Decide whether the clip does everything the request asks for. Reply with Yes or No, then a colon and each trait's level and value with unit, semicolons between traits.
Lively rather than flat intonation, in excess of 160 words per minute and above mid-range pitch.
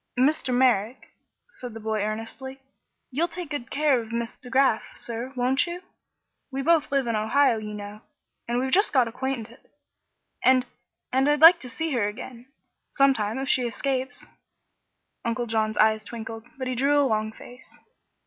No: average, 3.4 semitones; average, 170 wpm; very high, 250 Hz